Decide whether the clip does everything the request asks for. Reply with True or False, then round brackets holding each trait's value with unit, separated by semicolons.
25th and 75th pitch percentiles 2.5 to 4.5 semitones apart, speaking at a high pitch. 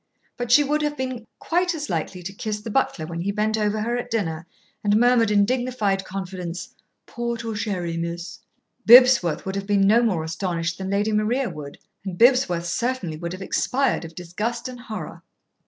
False (5.4 semitones; 210 Hz)